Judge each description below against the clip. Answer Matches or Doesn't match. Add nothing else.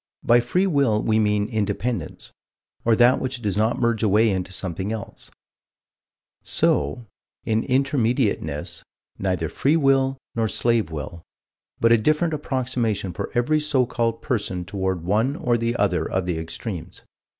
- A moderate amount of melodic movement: Matches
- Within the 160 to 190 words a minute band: Doesn't match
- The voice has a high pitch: Doesn't match